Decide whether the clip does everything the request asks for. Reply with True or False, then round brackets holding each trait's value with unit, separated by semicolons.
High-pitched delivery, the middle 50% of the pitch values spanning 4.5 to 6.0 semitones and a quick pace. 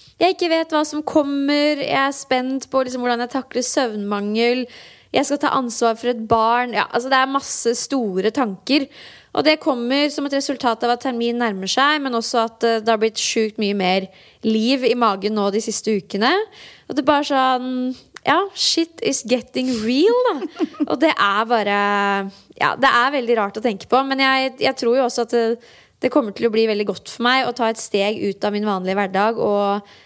False (245 Hz; 3.8 semitones; 210 wpm)